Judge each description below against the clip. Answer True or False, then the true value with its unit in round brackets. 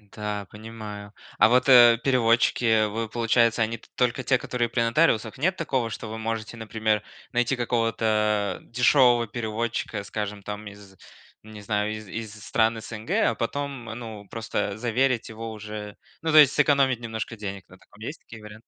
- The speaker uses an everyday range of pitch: False (2.1 semitones)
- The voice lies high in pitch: False (115 Hz)